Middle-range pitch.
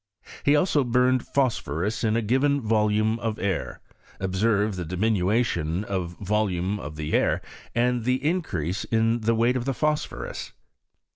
No: low, 110 Hz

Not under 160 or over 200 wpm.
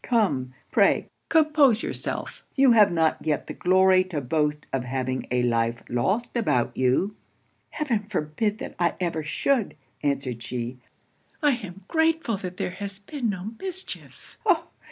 No: average, 150 wpm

